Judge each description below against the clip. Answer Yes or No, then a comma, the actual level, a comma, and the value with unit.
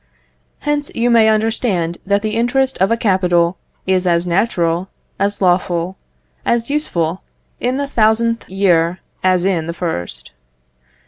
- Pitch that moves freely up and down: No, average, 5.0 semitones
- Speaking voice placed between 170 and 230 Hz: Yes, high, 190 Hz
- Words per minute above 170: No, slow, 135 wpm